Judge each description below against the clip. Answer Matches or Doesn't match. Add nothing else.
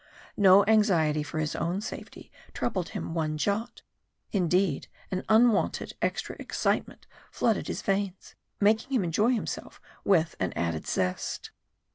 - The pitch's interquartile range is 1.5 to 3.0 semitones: Doesn't match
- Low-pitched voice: Doesn't match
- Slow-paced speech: Matches